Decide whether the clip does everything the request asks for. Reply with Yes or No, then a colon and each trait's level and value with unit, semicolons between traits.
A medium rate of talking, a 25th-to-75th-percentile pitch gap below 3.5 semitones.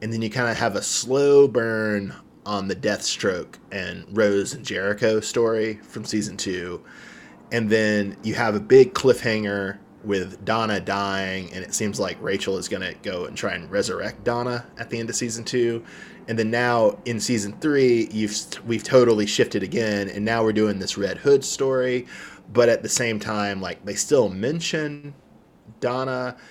Yes: average, 180 wpm; average, 3.0 semitones